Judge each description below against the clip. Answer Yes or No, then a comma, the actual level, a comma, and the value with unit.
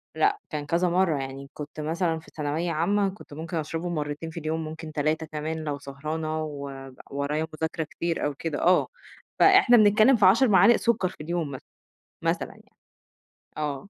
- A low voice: No, medium, 160 Hz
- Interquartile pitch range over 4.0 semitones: No, average, 3.1 semitones